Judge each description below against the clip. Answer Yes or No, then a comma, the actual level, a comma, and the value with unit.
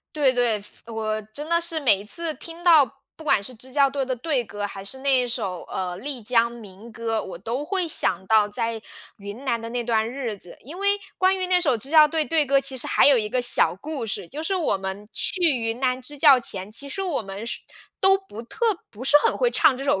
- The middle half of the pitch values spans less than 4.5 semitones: No, wide, 5.4 semitones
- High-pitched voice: Yes, very high, 250 Hz